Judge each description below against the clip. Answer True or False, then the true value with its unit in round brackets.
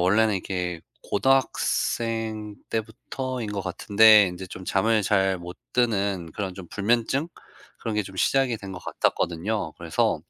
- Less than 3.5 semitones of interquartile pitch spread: True (3.1 semitones)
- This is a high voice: False (105 Hz)